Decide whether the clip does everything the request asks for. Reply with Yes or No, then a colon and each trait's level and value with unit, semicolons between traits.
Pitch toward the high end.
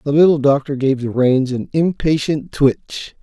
No: medium, 140 Hz